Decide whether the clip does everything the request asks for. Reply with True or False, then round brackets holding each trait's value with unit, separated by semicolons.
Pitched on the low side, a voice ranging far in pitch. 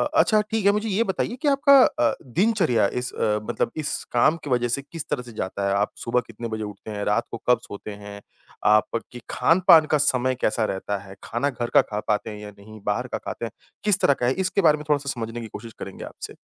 True (120 Hz; 6.4 semitones)